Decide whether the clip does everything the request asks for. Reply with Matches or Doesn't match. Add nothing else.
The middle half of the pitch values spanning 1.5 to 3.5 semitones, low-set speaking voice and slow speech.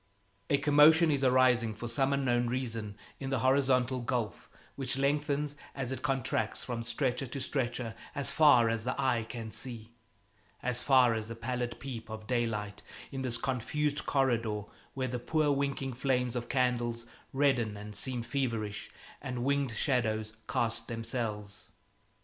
Doesn't match